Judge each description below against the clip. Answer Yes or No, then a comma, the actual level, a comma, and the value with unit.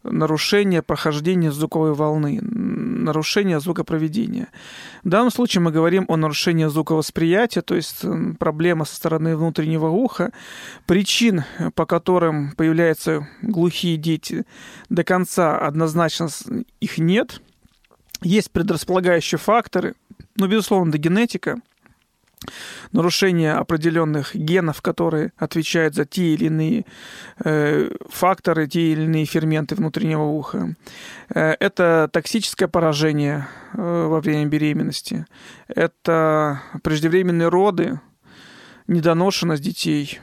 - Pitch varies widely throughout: No, average, 2.9 semitones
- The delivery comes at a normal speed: No, slow, 100 wpm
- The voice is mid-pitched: Yes, medium, 170 Hz